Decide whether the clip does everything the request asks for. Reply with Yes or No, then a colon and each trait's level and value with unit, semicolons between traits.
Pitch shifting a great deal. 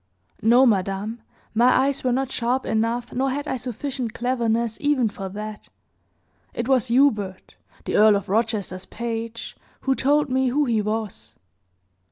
No: average, 3.3 semitones